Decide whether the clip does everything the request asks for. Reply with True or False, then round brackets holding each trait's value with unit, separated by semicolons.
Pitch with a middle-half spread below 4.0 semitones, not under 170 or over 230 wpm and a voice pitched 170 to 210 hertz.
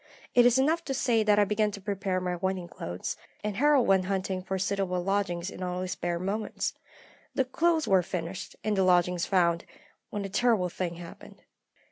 True (2.8 semitones; 190 wpm; 190 Hz)